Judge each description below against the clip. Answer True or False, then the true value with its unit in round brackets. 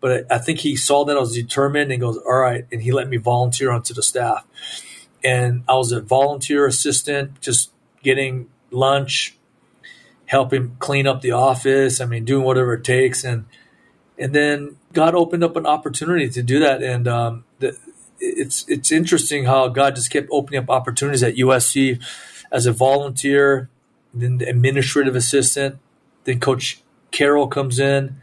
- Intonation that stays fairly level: True (1.9 semitones)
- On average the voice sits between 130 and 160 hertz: True (135 Hz)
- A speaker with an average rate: True (170 wpm)